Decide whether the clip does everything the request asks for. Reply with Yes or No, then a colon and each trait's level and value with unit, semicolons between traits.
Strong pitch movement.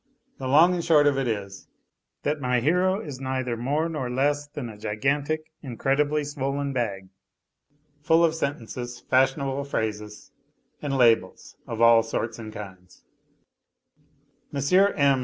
No: average, 4.0 semitones